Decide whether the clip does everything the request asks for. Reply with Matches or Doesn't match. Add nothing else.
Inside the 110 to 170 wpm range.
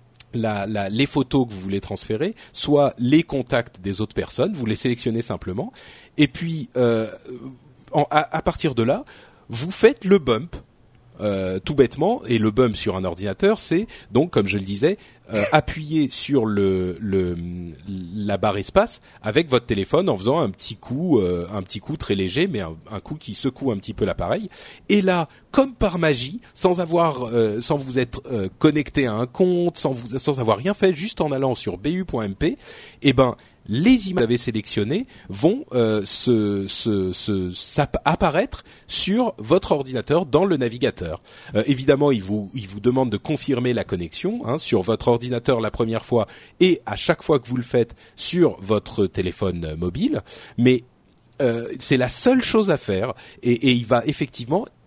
Doesn't match